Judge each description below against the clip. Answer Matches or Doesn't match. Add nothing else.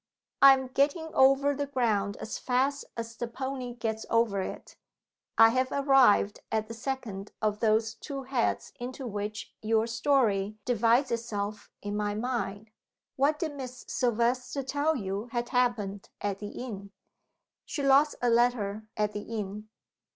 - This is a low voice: Doesn't match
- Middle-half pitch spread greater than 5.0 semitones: Doesn't match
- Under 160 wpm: Matches